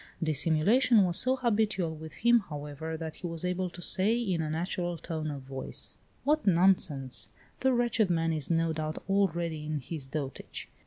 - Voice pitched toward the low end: No, medium, 165 Hz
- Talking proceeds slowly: No, average, 170 wpm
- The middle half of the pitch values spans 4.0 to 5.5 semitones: Yes, average, 4.3 semitones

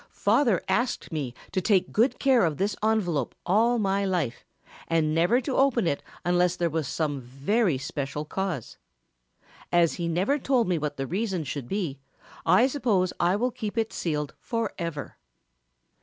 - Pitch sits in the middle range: Yes, medium, 180 Hz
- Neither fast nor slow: Yes, average, 160 wpm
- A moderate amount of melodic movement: No, wide, 6.3 semitones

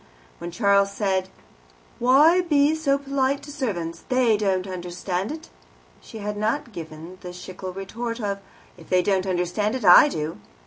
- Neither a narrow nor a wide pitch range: No, wide, 6.1 semitones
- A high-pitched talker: Yes, high, 200 Hz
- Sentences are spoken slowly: No, average, 160 wpm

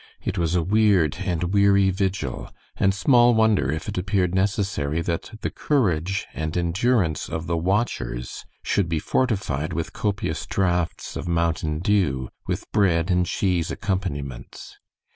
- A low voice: Yes, very low, 90 Hz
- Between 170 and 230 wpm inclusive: No, average, 140 wpm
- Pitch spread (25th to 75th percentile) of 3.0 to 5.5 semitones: Yes, average, 3.6 semitones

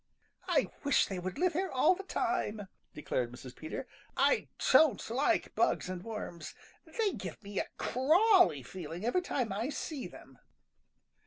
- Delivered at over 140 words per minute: Yes, average, 160 wpm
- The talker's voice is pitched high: Yes, high, 235 Hz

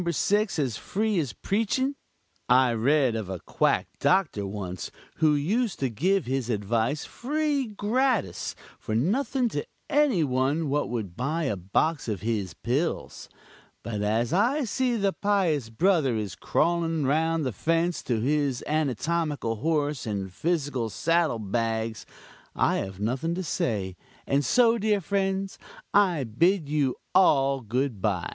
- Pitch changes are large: Yes, wide, 8.6 semitones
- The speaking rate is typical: Yes, average, 145 wpm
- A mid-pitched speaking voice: Yes, medium, 145 Hz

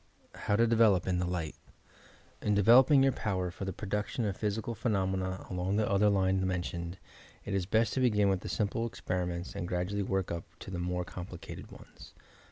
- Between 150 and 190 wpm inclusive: Yes, average, 185 wpm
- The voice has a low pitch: Yes, very low, 95 Hz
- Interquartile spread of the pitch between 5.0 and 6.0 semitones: No, average, 2.8 semitones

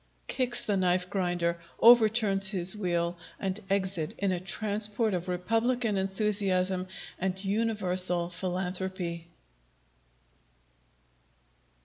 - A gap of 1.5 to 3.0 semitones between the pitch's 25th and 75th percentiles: Yes, average, 2.7 semitones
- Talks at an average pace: No, slow, 90 wpm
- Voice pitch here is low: No, high, 190 Hz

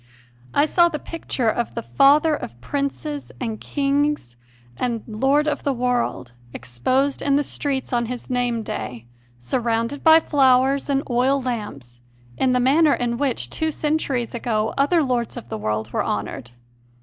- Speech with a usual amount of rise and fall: Yes, average, 4.0 semitones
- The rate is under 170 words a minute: Yes, average, 160 wpm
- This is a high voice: Yes, very high, 255 Hz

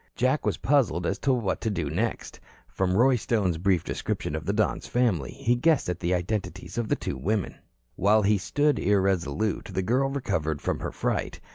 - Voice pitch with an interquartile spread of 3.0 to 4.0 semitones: No, average, 5.1 semitones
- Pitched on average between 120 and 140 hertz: No, low, 100 Hz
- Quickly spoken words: No, average, 190 wpm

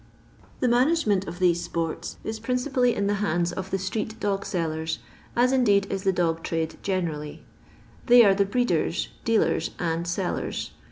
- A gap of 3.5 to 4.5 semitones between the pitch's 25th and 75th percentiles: No, average, 4.9 semitones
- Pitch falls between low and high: No, high, 195 Hz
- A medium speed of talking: Yes, average, 160 wpm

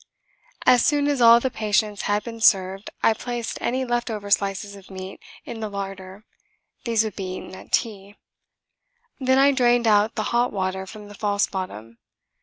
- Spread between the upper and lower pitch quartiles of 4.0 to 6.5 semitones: No, average, 3.4 semitones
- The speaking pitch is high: Yes, high, 210 Hz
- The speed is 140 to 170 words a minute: No, average, 180 wpm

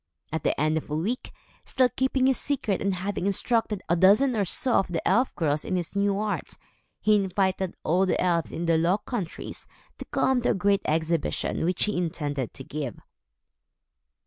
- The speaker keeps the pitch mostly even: No, average, 4.3 semitones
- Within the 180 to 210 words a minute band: Yes, average, 190 wpm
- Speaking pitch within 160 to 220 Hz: Yes, high, 190 Hz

